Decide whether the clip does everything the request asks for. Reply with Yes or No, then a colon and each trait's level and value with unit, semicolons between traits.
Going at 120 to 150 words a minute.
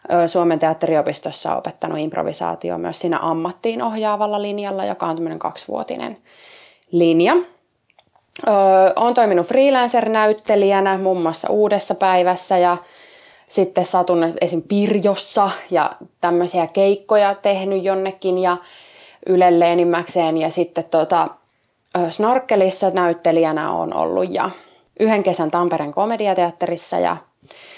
No: average, 100 wpm